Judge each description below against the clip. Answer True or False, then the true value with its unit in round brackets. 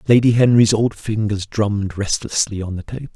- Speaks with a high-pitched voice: False (105 Hz)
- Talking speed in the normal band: True (170 wpm)